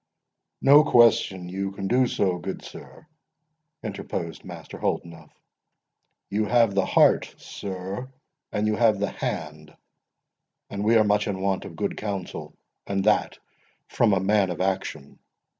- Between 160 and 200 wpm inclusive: No, average, 140 wpm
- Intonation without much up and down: Yes, narrow, 2.3 semitones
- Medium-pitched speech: No, low, 100 Hz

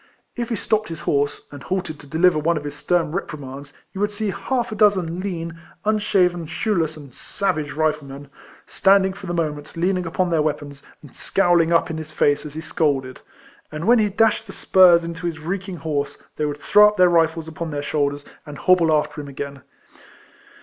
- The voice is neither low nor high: Yes, medium, 165 Hz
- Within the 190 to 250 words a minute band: Yes, average, 200 wpm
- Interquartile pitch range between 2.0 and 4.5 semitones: Yes, average, 4.1 semitones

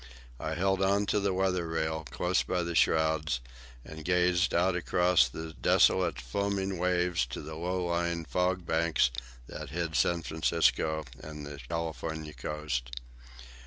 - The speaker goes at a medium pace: Yes, average, 145 wpm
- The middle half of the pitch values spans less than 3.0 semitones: Yes, narrow, 2.5 semitones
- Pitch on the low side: Yes, very low, 85 Hz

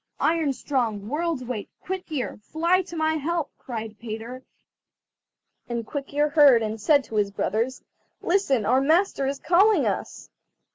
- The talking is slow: No, average, 150 wpm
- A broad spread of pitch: Yes, wide, 5.9 semitones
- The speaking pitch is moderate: No, very high, 275 Hz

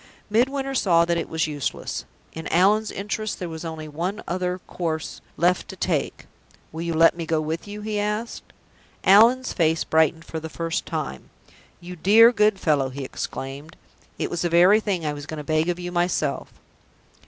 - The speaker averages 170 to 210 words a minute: Yes, average, 185 wpm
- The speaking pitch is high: No, medium, 170 Hz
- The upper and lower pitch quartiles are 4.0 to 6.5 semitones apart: Yes, average, 4.4 semitones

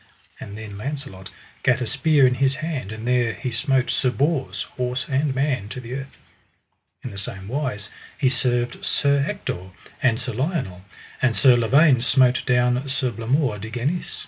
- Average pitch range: Yes, average, 3.2 semitones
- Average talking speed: Yes, average, 170 wpm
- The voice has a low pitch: Yes, low, 125 Hz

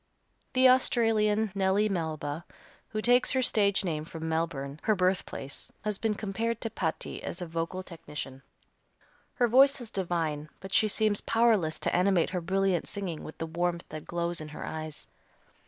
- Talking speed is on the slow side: No, average, 165 wpm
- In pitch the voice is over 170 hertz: Yes, medium, 185 Hz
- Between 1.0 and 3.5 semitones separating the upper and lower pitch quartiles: No, average, 4.9 semitones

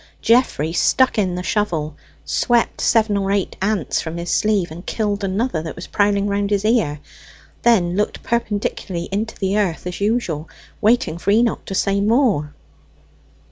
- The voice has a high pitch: Yes, high, 200 Hz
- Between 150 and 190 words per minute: Yes, average, 160 wpm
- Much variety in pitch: No, average, 3.8 semitones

